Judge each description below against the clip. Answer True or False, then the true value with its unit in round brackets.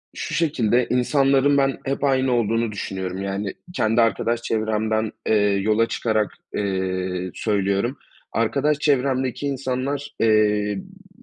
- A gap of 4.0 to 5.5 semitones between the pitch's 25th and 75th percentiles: True (4.6 semitones)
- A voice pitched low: True (115 Hz)